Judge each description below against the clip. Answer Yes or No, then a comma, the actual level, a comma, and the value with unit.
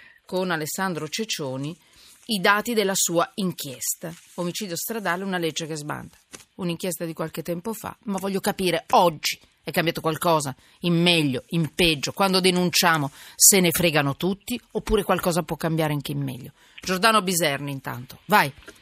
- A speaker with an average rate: Yes, average, 150 wpm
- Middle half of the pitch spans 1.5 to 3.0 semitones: No, average, 3.5 semitones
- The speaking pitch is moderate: Yes, medium, 170 Hz